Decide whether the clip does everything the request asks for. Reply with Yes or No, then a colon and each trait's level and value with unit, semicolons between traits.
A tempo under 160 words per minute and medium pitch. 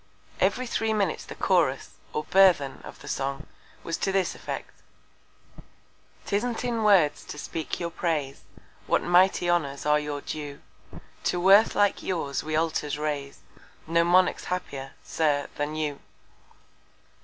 Yes: average, 140 wpm; medium, 165 Hz